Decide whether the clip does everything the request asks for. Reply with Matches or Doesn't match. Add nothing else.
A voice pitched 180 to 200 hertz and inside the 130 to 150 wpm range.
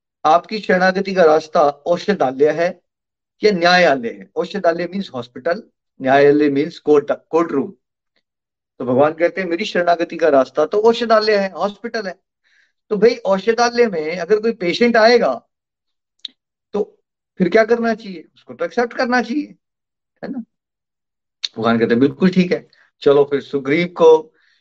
Matches